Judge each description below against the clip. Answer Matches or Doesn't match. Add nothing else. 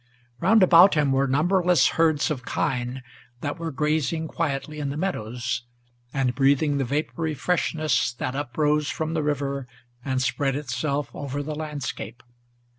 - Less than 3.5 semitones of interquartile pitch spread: Matches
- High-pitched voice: Doesn't match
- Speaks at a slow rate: Doesn't match